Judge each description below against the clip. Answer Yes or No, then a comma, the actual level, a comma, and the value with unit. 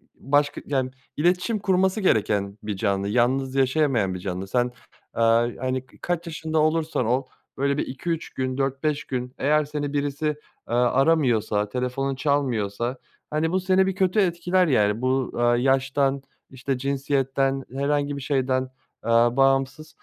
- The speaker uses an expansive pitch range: No, average, 3.4 semitones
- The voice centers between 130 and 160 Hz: Yes, low, 135 Hz